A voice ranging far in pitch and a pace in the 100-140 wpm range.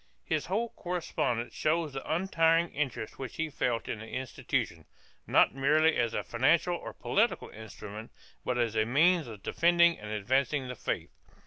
No: wide, 6.1 semitones; average, 165 wpm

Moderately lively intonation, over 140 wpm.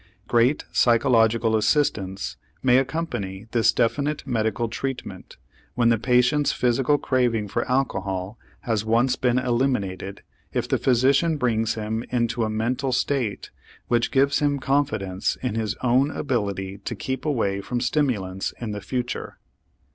No: average, 3.5 semitones; slow, 135 wpm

